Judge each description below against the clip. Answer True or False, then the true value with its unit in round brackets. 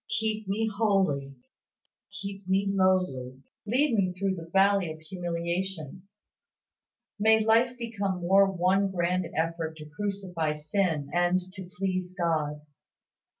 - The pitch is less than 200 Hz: True (185 Hz)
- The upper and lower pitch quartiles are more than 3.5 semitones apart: False (2.9 semitones)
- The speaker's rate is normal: False (120 wpm)